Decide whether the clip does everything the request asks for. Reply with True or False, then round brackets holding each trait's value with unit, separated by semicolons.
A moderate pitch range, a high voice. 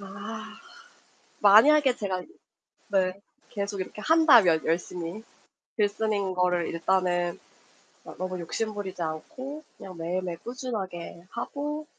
True (3.9 semitones; 195 Hz)